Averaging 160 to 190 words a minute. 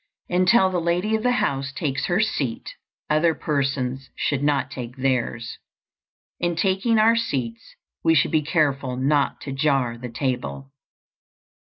No: average, 145 wpm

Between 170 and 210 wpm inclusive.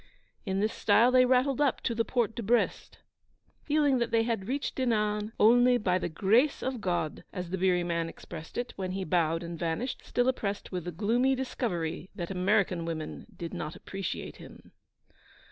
Yes: average, 180 wpm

